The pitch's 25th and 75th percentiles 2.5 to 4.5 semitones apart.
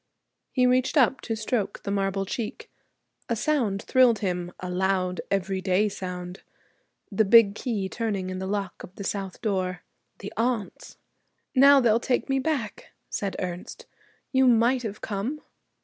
Yes: average, 4.2 semitones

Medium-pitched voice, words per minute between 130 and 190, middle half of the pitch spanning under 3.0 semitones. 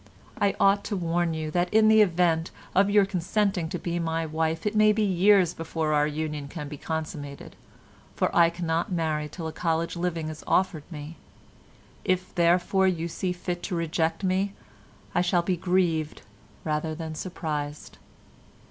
Yes: medium, 170 Hz; average, 165 wpm; narrow, 2.6 semitones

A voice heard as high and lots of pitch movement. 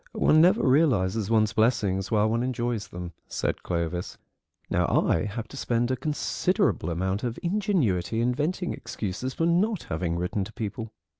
No: low, 115 Hz; wide, 6.7 semitones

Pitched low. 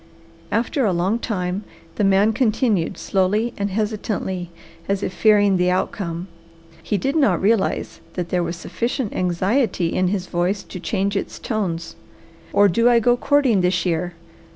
No: high, 195 Hz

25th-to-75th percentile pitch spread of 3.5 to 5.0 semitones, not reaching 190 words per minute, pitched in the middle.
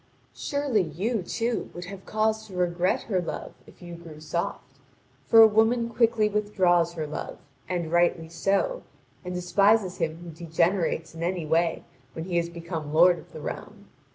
Yes: average, 3.9 semitones; average, 170 wpm; medium, 175 Hz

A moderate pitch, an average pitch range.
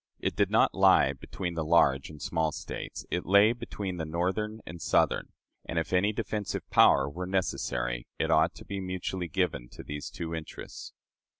No: very low, 85 Hz; average, 3.5 semitones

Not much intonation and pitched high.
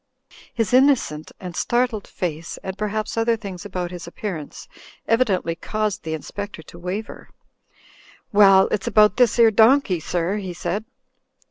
No: average, 3.9 semitones; high, 200 Hz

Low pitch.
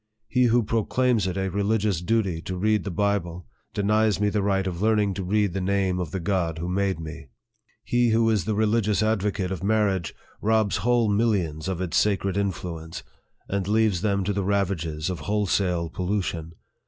Yes: low, 100 Hz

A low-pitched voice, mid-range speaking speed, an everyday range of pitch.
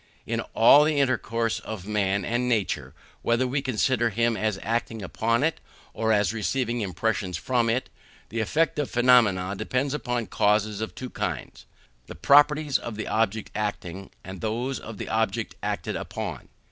Yes: low, 115 Hz; average, 160 wpm; average, 3.3 semitones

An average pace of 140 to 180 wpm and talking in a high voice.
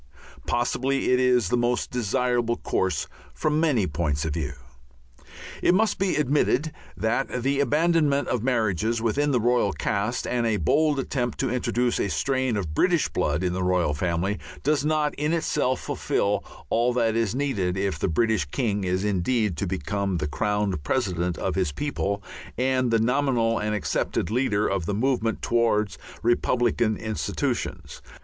No: average, 160 wpm; low, 115 Hz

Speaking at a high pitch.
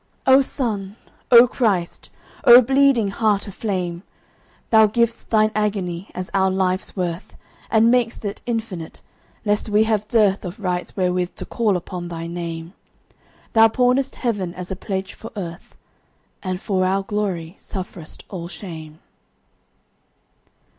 Yes: high, 195 Hz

